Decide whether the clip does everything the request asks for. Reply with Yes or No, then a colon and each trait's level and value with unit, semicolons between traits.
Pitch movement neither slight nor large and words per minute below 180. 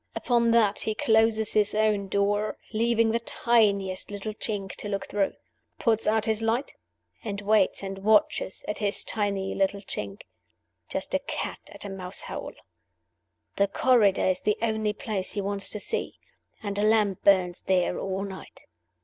No: narrow, 1.9 semitones; average, 165 wpm